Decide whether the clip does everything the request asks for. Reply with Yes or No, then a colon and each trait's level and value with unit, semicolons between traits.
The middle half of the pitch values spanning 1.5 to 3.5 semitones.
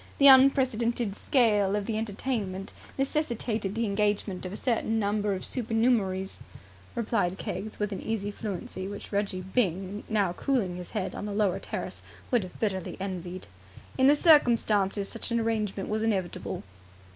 Yes: average, 3.1 semitones